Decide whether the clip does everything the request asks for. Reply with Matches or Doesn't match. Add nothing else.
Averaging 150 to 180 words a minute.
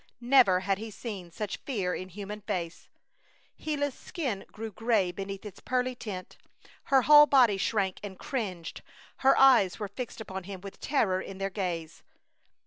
Matches